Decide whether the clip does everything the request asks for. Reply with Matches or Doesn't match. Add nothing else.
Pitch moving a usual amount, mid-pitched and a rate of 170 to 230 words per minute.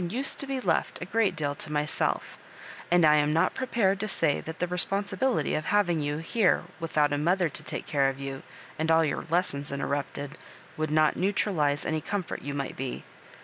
Matches